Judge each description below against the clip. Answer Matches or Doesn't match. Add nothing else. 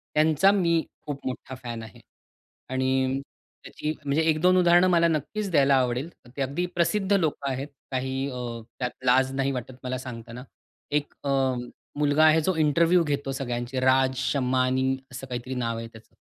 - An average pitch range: Matches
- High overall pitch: Doesn't match